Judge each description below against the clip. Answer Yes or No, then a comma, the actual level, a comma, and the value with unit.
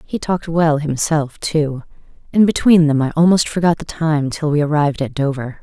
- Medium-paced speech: Yes, average, 190 wpm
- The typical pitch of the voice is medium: Yes, medium, 155 Hz